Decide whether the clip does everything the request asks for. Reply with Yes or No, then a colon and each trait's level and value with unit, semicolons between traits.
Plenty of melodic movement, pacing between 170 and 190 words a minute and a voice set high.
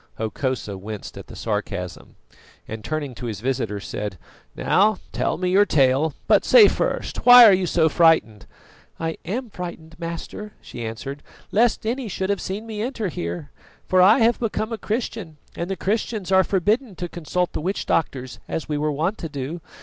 No: wide, 7.4 semitones; average, 180 wpm; medium, 170 Hz